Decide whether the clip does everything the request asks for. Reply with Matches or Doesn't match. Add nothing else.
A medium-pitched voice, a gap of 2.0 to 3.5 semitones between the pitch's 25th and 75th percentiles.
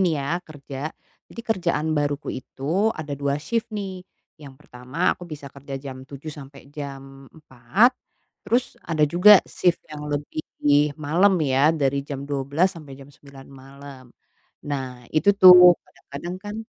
Doesn't match